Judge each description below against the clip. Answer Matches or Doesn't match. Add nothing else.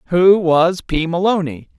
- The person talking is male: Matches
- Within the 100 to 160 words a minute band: Matches